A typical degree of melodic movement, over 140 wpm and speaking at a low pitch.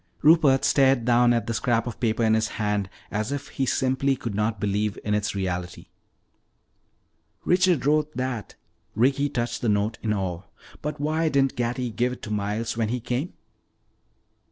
Yes: average, 4.2 semitones; average, 170 wpm; low, 120 Hz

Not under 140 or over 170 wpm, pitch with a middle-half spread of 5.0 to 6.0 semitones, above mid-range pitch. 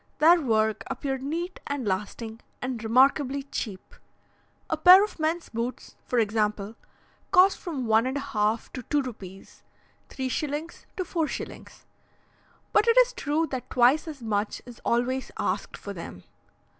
Yes: average, 145 wpm; wide, 5.6 semitones; very high, 260 Hz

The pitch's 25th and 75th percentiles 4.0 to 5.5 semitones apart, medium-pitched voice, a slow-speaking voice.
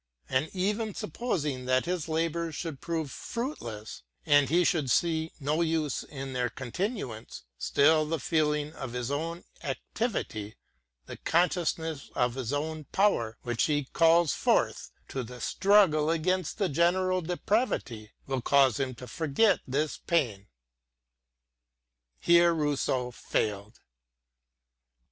Yes: average, 4.7 semitones; medium, 155 Hz; slow, 120 wpm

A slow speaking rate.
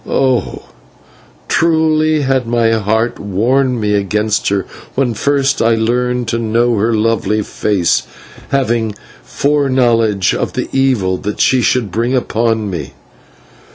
Yes: slow, 125 wpm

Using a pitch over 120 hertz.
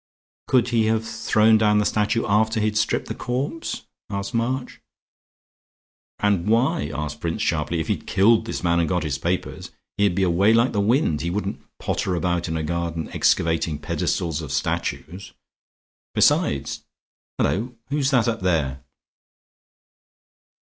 No: low, 100 Hz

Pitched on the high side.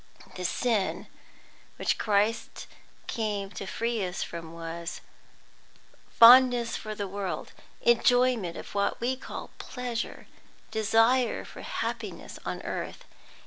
Yes: high, 220 Hz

